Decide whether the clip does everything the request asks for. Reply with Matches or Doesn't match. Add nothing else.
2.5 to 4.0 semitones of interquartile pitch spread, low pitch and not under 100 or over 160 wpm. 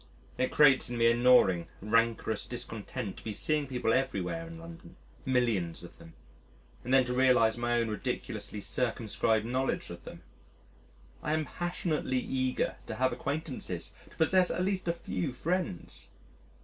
Doesn't match